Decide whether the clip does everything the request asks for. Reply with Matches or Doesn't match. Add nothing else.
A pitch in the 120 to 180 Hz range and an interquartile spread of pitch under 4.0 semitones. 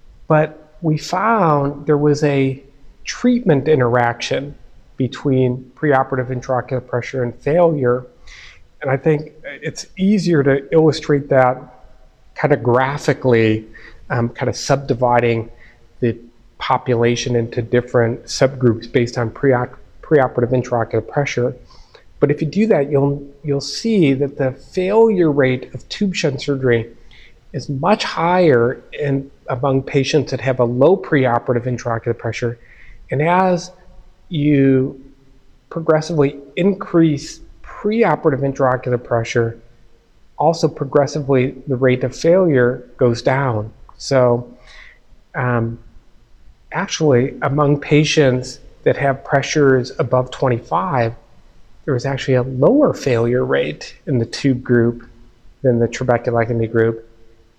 Matches